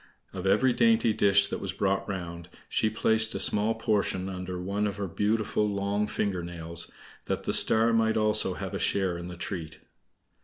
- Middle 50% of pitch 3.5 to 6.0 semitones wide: No, average, 2.9 semitones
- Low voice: Yes, low, 100 Hz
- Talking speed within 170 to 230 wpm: Yes, average, 185 wpm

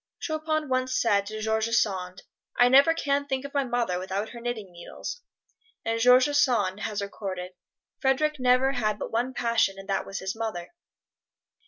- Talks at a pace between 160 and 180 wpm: Yes, average, 170 wpm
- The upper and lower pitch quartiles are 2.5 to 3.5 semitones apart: No, average, 4.8 semitones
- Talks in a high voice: Yes, high, 235 Hz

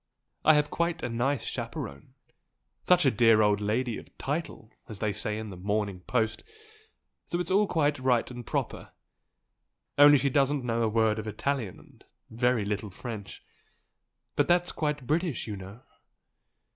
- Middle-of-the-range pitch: No, low, 120 Hz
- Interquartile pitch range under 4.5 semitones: No, average, 5.3 semitones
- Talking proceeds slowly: No, average, 165 wpm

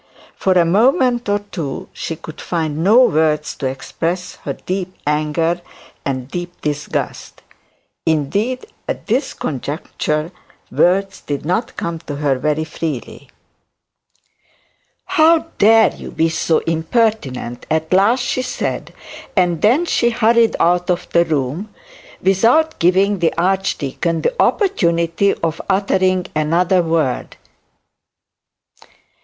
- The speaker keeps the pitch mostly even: No, average, 4.6 semitones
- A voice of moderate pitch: Yes, medium, 175 Hz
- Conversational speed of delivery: No, slow, 120 wpm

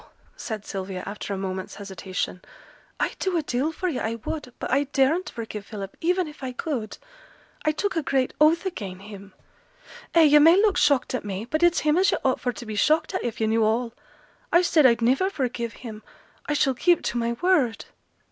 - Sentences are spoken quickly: Yes, fast, 210 wpm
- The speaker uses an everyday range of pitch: No, wide, 6.6 semitones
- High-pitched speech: Yes, very high, 255 Hz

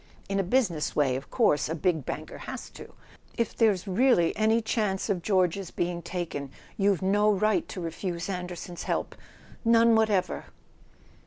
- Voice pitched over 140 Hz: Yes, high, 190 Hz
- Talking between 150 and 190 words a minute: Yes, average, 155 wpm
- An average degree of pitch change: Yes, average, 3.8 semitones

